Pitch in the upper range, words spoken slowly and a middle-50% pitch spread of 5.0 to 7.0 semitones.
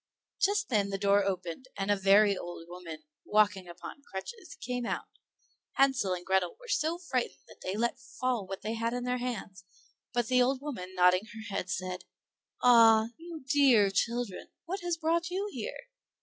No: high, 220 Hz; average, 180 wpm; wide, 5.5 semitones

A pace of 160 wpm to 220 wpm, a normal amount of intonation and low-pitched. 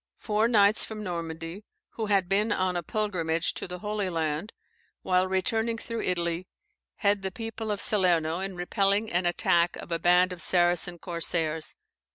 No: average, 165 wpm; average, 3.3 semitones; medium, 185 Hz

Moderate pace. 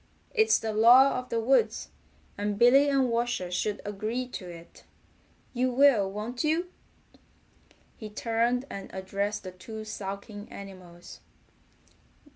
No: slow, 125 wpm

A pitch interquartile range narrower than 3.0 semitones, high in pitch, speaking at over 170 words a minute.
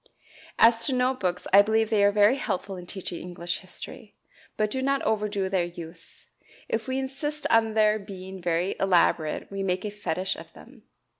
No: average, 3.5 semitones; high, 205 Hz; average, 180 wpm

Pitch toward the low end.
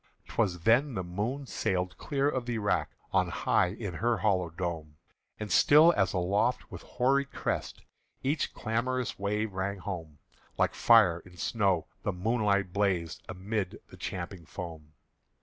Yes: low, 100 Hz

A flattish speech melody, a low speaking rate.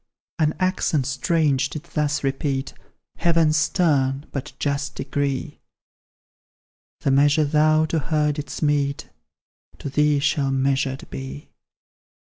Yes: narrow, 2.1 semitones; slow, 110 wpm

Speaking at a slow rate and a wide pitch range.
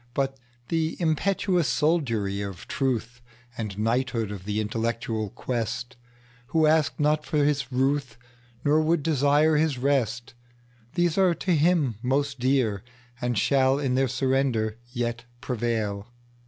No: slow, 115 wpm; average, 3.7 semitones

